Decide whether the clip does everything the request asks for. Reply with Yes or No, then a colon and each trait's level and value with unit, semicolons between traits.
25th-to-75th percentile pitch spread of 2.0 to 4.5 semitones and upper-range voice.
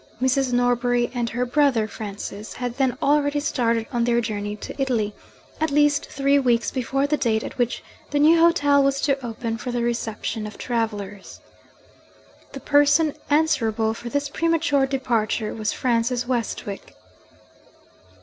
Yes: average, 3.8 semitones; high, 245 Hz